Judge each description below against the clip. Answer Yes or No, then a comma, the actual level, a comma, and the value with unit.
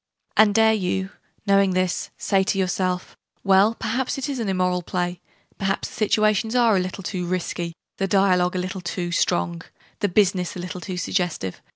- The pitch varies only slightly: Yes, narrow, 2.2 semitones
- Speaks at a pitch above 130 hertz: Yes, high, 190 Hz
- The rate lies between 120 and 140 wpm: No, average, 180 wpm